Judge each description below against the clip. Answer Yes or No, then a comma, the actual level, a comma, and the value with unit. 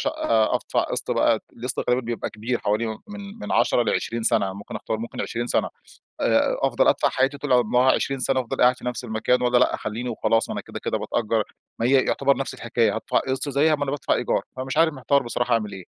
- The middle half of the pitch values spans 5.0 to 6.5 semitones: No, average, 3.0 semitones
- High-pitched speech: No, low, 125 Hz